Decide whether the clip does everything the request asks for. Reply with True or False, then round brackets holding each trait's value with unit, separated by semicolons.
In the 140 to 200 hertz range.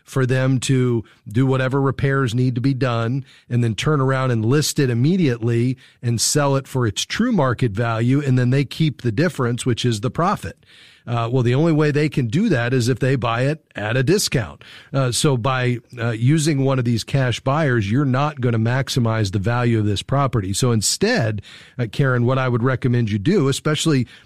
False (130 Hz)